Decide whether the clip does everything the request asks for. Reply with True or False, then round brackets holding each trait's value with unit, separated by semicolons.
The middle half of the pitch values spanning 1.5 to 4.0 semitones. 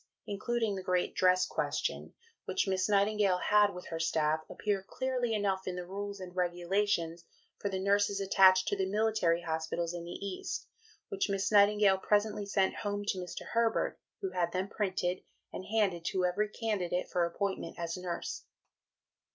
True (2.4 semitones)